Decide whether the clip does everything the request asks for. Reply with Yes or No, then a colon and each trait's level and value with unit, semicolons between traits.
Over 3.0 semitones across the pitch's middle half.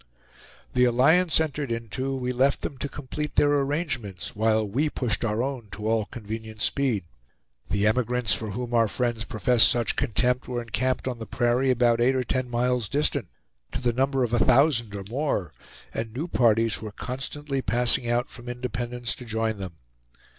No: narrow, 2.6 semitones